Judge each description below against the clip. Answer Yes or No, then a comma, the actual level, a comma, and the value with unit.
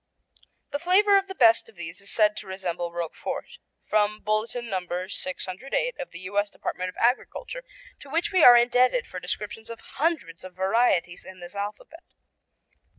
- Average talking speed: Yes, average, 165 wpm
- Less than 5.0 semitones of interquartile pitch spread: No, wide, 5.6 semitones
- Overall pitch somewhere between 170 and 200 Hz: No, high, 215 Hz